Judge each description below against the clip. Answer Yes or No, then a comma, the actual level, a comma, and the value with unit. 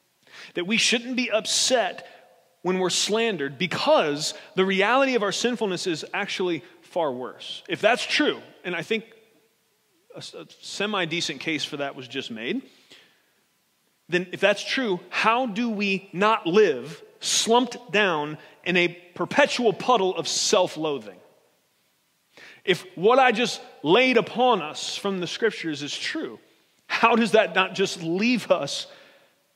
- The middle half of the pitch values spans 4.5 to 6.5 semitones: Yes, average, 5.3 semitones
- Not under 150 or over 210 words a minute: No, average, 140 wpm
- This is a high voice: Yes, high, 200 Hz